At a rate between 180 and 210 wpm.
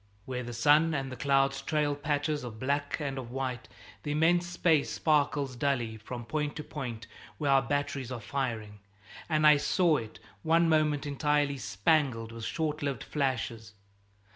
No: average, 165 wpm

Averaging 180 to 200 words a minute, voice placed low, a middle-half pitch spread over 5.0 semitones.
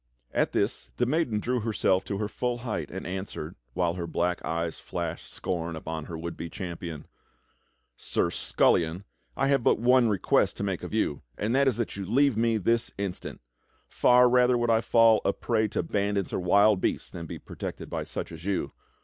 Yes: average, 195 wpm; low, 100 Hz; wide, 5.4 semitones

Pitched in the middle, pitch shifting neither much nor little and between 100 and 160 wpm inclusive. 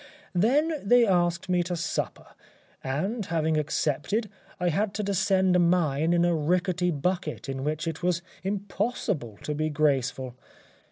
Yes: medium, 175 Hz; average, 4.0 semitones; average, 150 wpm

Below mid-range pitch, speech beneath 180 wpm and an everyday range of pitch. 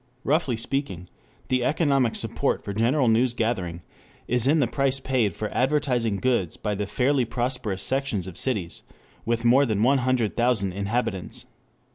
Yes: low, 120 Hz; average, 155 wpm; average, 4.2 semitones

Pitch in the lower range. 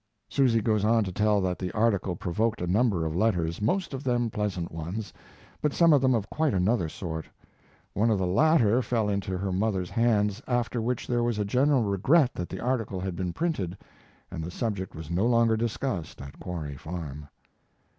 Yes: low, 105 Hz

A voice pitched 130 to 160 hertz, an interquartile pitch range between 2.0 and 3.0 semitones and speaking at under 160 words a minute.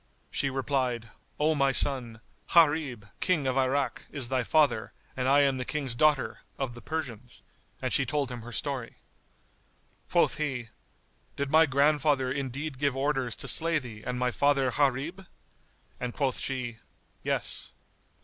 Yes: low, 135 Hz; narrow, 2.6 semitones; average, 150 wpm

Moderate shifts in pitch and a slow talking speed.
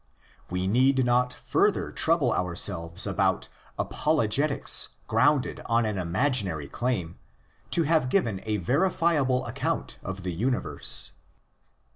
No: wide, 6.6 semitones; slow, 110 wpm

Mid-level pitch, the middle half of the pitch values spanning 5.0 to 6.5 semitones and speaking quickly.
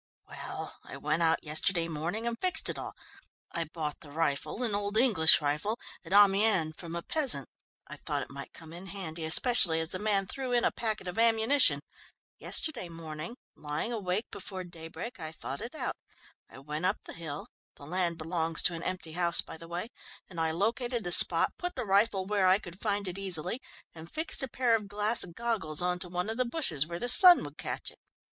Yes: medium, 180 Hz; average, 5.3 semitones; fast, 210 wpm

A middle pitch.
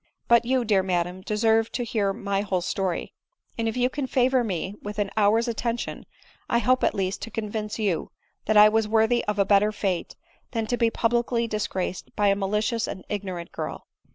No: high, 215 Hz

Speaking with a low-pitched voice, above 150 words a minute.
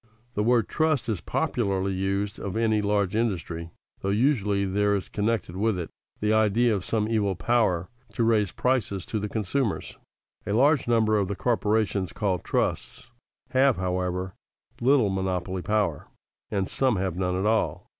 Yes: low, 105 Hz; average, 160 wpm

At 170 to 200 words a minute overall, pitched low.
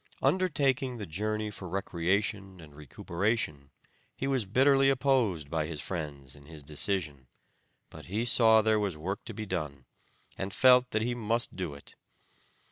No: average, 155 wpm; low, 100 Hz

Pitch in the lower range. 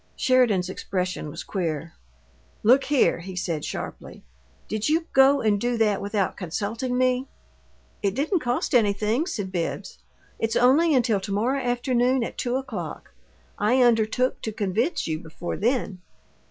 No: high, 225 Hz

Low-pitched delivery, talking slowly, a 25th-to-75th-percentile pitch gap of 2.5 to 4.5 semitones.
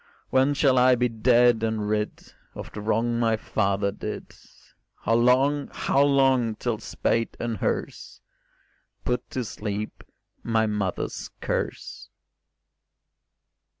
Yes: low, 115 Hz; slow, 115 wpm; average, 2.8 semitones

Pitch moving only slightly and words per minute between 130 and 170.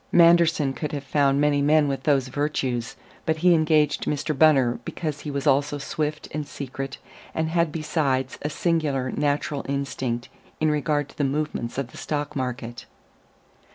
Yes: narrow, 2.2 semitones; average, 160 wpm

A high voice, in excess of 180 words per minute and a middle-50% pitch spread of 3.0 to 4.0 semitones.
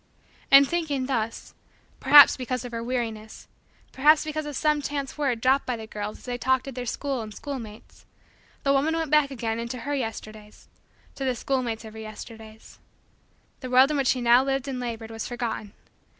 Yes: very high, 255 Hz; average, 190 wpm; average, 3.6 semitones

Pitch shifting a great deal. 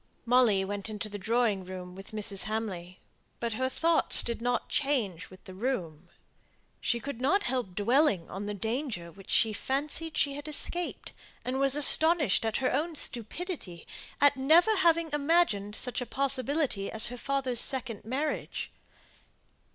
Yes: wide, 5.8 semitones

